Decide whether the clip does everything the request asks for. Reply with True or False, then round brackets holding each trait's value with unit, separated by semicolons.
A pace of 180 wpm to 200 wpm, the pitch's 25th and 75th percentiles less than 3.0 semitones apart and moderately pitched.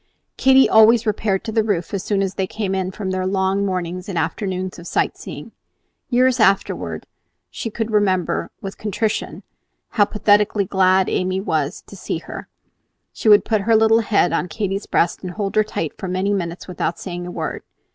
False (190 wpm; 2.6 semitones; 195 Hz)